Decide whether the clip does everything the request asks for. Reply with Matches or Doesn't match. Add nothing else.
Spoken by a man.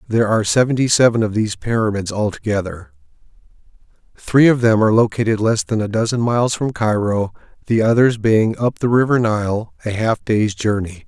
Matches